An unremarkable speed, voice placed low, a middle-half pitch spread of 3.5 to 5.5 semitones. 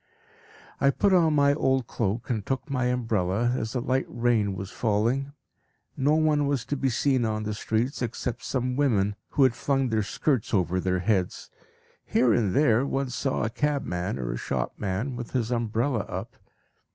Yes: average, 175 wpm; low, 120 Hz; average, 4.1 semitones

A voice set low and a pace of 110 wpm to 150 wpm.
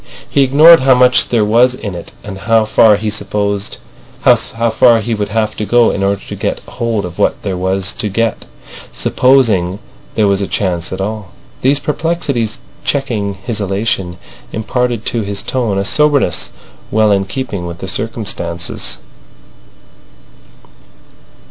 Yes: low, 110 Hz; average, 140 wpm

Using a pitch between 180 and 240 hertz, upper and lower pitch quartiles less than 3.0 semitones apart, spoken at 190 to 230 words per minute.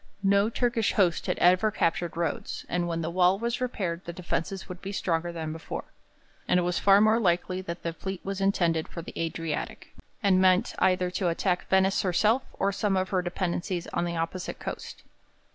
Yes: medium, 185 Hz; narrow, 2.4 semitones; average, 195 wpm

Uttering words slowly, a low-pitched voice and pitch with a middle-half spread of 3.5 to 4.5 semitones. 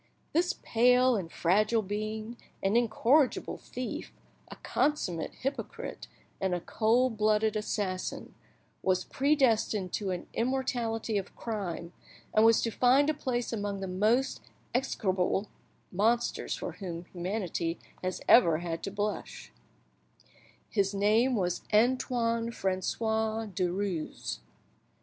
No: slow, 115 wpm; high, 215 Hz; average, 4.0 semitones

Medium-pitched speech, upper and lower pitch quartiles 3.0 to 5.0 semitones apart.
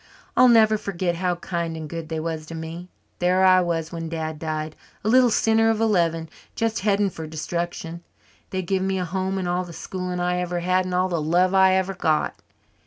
No: medium, 180 Hz; narrow, 2.4 semitones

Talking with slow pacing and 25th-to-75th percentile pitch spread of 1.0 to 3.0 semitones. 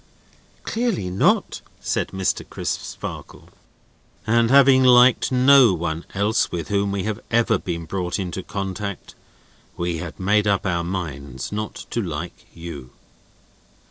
No: slow, 130 wpm; average, 4.5 semitones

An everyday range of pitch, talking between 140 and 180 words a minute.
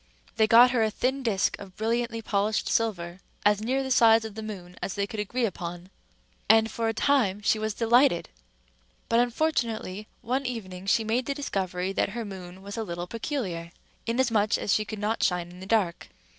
No: average, 3.4 semitones; average, 195 wpm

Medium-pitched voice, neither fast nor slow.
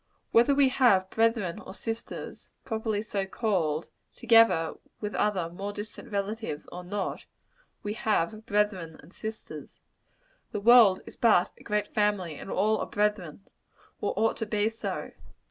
No: high, 210 Hz; average, 145 wpm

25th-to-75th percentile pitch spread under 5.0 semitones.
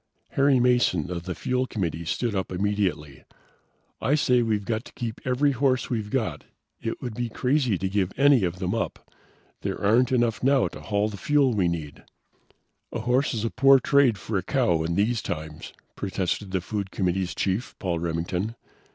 No: wide, 5.4 semitones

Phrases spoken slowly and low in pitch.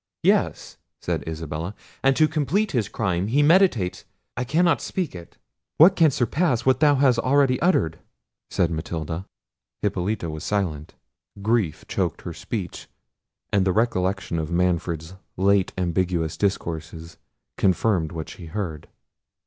Yes: slow, 130 wpm; very low, 95 Hz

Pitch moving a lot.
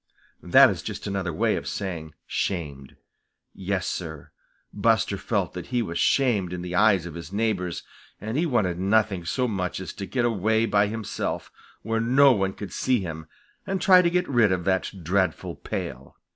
No: average, 4.2 semitones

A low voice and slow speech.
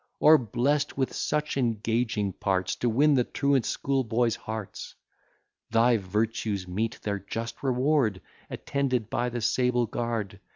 Yes: low, 115 Hz; slow, 130 wpm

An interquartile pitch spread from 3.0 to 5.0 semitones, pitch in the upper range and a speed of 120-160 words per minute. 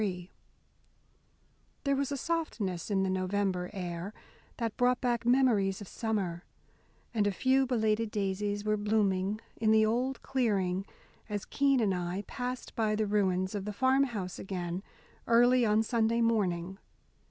Yes: average, 3.9 semitones; high, 210 Hz; average, 150 wpm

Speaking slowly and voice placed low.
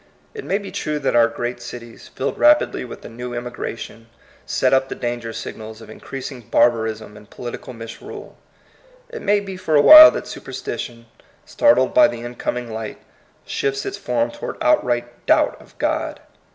No: average, 165 wpm; low, 120 Hz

